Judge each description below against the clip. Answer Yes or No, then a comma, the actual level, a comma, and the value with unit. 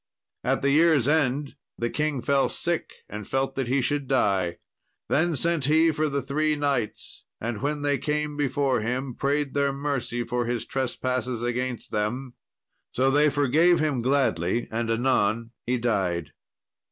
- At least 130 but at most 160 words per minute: Yes, average, 155 wpm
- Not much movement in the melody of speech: No, average, 3.4 semitones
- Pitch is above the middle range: No, low, 135 Hz